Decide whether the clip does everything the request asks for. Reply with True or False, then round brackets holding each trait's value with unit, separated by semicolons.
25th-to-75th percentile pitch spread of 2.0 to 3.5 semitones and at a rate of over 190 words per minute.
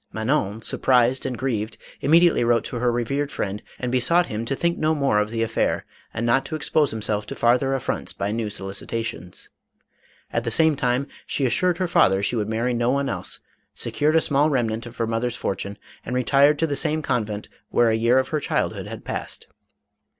False (3.9 semitones; 200 wpm)